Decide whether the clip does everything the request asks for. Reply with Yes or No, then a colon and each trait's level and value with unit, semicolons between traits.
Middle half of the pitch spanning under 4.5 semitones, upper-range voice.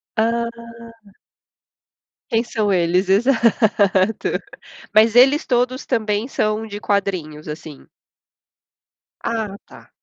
Yes: average, 3.2 semitones; high, 215 Hz